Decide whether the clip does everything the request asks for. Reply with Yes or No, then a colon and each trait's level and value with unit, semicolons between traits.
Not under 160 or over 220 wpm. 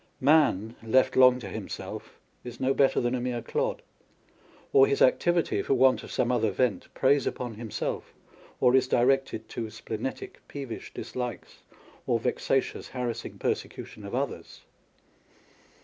No: average, 140 wpm